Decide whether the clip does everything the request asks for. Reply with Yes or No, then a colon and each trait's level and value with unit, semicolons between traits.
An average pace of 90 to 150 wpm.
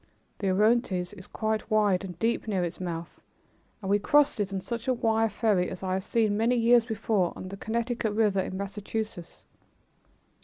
No: average, 190 wpm